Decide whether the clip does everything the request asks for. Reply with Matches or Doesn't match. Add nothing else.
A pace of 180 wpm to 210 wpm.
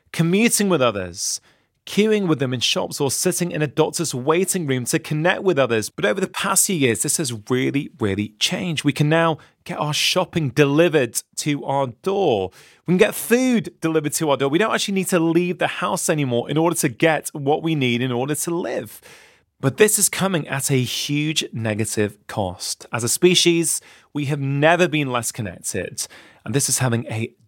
Matches